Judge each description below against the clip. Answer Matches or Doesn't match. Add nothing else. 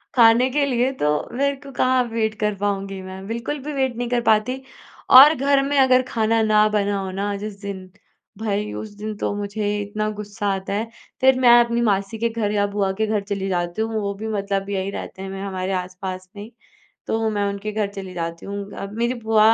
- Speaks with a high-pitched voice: Matches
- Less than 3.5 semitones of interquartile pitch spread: Matches